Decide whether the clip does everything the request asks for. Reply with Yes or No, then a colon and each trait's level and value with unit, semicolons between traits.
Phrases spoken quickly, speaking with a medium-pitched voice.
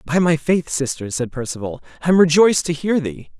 Yes: fast, 210 wpm; medium, 155 Hz